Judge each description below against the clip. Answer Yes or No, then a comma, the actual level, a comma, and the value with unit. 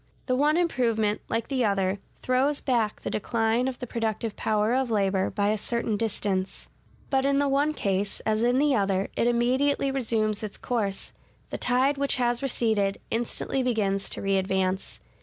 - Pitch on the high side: Yes, high, 230 Hz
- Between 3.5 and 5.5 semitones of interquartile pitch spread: Yes, average, 4.1 semitones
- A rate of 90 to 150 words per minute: No, average, 170 wpm